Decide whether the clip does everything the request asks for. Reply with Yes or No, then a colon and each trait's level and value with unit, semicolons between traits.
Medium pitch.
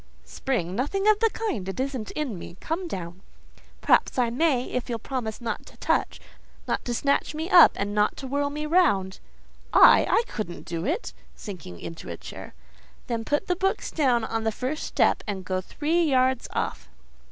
No: very high, 250 Hz